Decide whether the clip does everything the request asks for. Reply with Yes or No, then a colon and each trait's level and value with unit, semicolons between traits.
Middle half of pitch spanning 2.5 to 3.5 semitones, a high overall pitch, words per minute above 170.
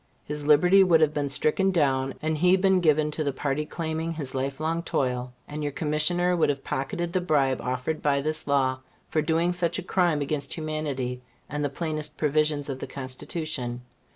No: average, 2.8 semitones; medium, 150 Hz; average, 190 wpm